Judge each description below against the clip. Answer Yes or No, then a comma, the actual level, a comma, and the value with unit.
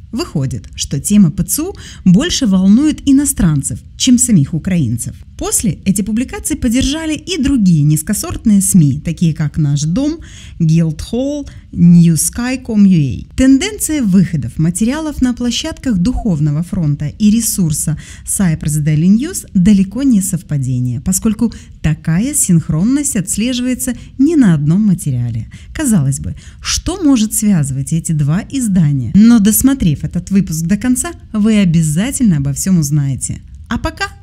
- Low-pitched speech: No, high, 195 Hz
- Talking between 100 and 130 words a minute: Yes, average, 120 wpm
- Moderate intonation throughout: No, wide, 7.9 semitones